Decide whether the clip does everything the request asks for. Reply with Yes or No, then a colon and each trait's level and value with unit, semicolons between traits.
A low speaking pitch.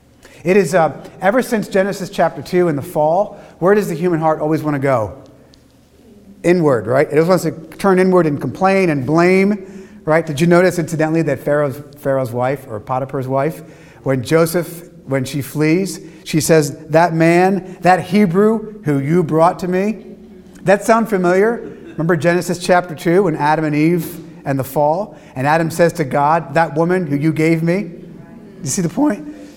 No: medium, 170 Hz